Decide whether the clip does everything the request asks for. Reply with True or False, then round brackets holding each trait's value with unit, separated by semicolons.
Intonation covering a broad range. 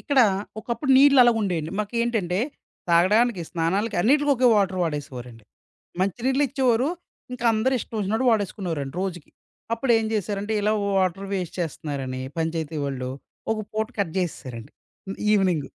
True (5.9 semitones)